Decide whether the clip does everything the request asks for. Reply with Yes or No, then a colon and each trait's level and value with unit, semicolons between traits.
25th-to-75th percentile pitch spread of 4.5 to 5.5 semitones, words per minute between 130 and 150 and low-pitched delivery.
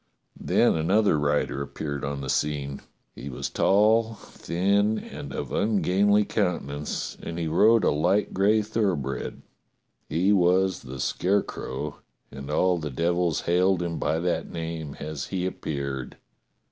Yes: average, 5.2 semitones; slow, 135 wpm; very low, 85 Hz